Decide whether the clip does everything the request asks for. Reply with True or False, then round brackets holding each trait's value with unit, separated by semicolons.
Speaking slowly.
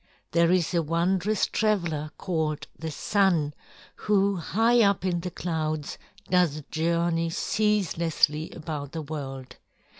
True (120 wpm)